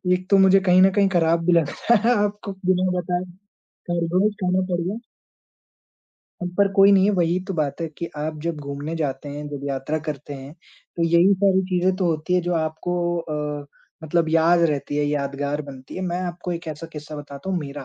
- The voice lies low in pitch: No, medium, 170 Hz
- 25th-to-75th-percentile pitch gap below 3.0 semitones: No, average, 3.8 semitones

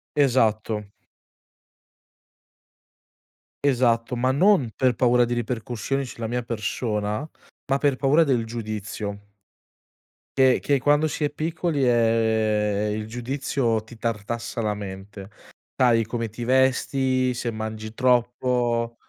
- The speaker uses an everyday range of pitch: Yes, average, 3.1 semitones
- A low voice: Yes, low, 120 Hz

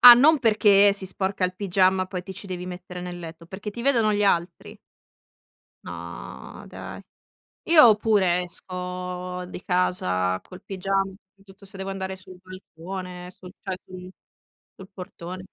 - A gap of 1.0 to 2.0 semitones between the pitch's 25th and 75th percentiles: Yes, narrow, 1.5 semitones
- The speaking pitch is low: No, medium, 185 Hz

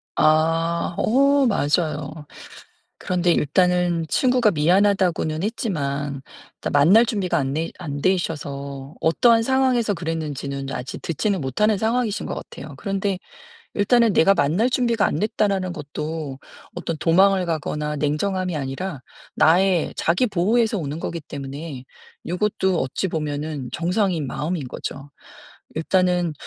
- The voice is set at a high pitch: No, medium, 170 Hz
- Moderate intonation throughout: Yes, average, 5.0 semitones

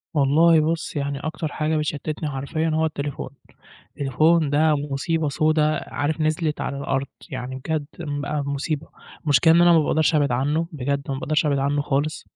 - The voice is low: No, medium, 150 Hz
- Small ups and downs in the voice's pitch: Yes, narrow, 1.9 semitones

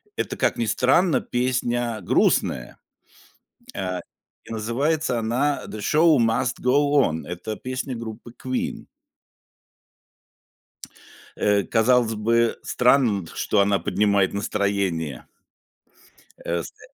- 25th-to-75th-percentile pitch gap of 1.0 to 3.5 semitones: No, average, 3.9 semitones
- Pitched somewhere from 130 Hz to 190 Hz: No, low, 115 Hz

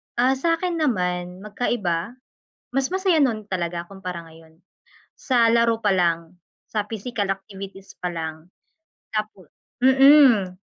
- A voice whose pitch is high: Yes, high, 200 Hz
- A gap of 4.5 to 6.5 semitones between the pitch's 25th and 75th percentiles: Yes, wide, 5.6 semitones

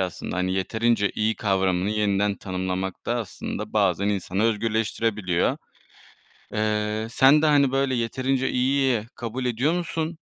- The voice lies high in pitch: No, low, 110 Hz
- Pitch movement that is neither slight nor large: Yes, average, 4.7 semitones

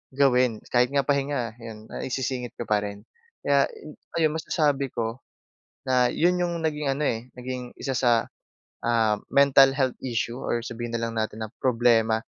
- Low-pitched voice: Yes, low, 125 Hz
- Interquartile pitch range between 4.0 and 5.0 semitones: No, average, 3.2 semitones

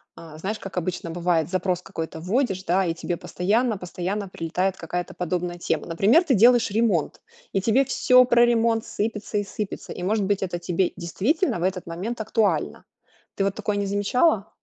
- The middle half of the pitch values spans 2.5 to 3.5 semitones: No, average, 4.0 semitones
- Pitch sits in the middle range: No, high, 195 Hz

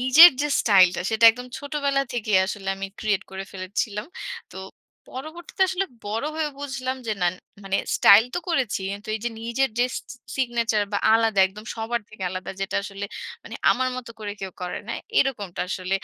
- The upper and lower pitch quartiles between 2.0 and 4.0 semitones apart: No, average, 4.7 semitones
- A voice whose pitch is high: Yes, high, 225 Hz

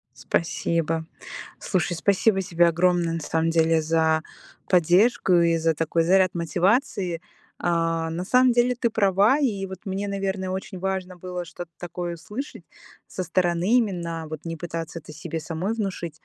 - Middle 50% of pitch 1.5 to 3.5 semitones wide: Yes, average, 2.8 semitones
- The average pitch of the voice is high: No, medium, 175 Hz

